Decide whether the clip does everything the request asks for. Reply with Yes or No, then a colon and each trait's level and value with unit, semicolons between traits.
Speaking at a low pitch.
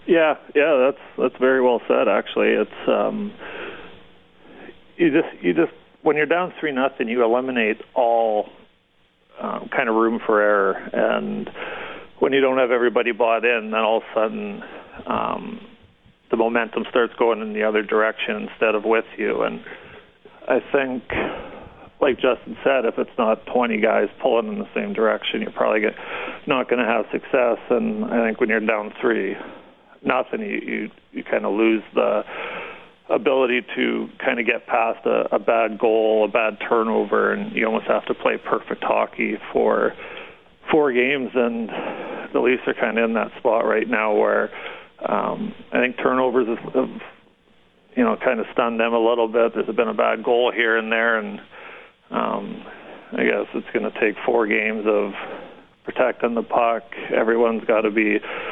Yes: low, 120 Hz